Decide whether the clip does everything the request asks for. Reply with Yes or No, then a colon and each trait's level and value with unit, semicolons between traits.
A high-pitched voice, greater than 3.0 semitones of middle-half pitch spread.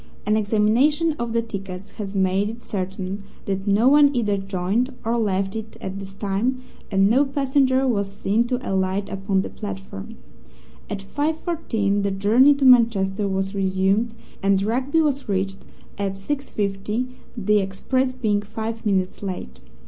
Yes: high, 205 Hz; average, 4.0 semitones